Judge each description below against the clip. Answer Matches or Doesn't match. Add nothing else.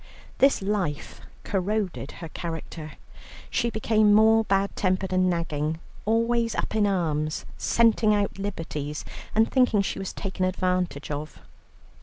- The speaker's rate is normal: Doesn't match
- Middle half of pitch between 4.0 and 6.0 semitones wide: Matches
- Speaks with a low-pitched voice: Doesn't match